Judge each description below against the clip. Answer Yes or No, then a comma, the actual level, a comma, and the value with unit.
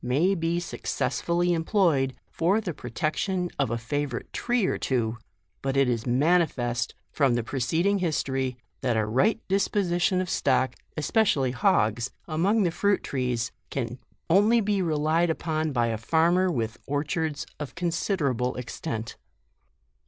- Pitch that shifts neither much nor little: No, wide, 6.0 semitones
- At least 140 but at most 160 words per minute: Yes, average, 145 wpm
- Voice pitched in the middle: Yes, medium, 155 Hz